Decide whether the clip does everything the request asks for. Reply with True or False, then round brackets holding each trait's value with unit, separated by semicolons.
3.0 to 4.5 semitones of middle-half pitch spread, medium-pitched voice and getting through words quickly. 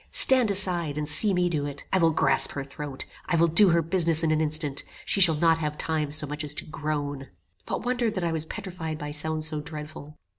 False (2.5 semitones; 160 Hz; 230 wpm)